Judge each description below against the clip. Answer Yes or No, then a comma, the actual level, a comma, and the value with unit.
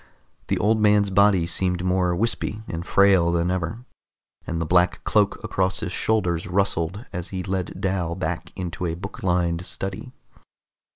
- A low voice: Yes, very low, 90 Hz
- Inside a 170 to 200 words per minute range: No, average, 160 wpm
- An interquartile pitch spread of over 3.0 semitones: No, narrow, 2.4 semitones